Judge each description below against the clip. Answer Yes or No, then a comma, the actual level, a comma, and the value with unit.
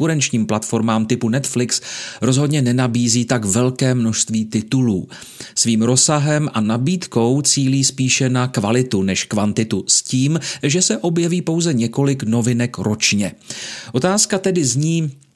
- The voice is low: Yes, low, 125 Hz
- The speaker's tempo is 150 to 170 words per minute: No, average, 125 wpm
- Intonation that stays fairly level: No, average, 4.5 semitones